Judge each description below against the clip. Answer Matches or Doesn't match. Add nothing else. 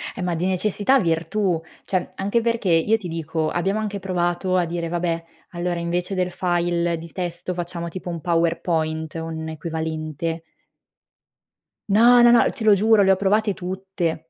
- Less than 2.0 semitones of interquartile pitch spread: Doesn't match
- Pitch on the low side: Doesn't match